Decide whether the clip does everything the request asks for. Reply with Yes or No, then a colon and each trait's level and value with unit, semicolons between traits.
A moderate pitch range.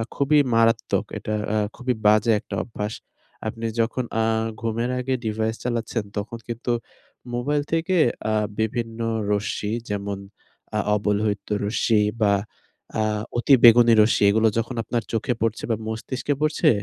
No: narrow, 2.2 semitones